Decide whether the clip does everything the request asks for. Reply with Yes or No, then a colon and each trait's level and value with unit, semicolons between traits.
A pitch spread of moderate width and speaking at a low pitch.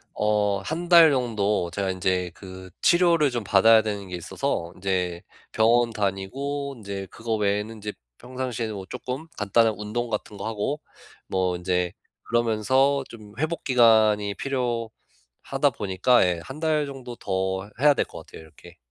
Yes: average, 4.9 semitones; low, 110 Hz